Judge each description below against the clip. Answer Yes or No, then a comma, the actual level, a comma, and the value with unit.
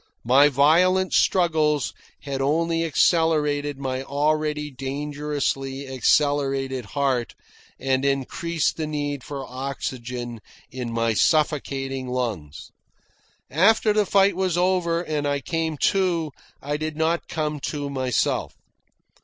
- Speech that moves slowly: Yes, slow, 110 wpm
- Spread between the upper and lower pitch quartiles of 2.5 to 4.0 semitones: Yes, average, 3.2 semitones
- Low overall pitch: No, medium, 145 Hz